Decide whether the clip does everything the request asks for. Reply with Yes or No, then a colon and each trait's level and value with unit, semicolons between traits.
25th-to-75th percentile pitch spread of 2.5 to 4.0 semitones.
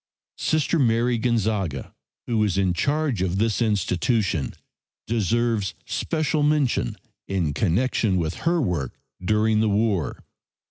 No: average, 4.4 semitones